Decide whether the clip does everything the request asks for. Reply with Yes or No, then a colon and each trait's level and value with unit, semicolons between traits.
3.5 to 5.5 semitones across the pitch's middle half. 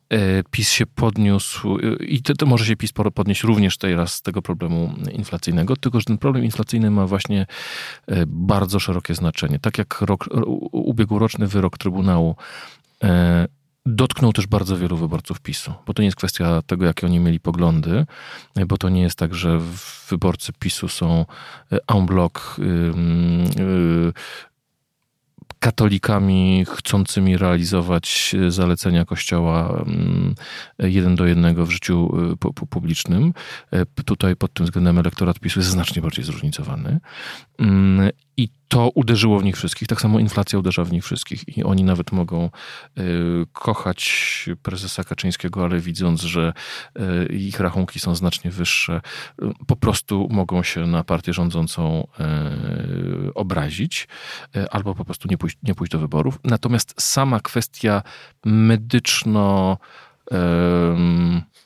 Yes: average, 4.0 semitones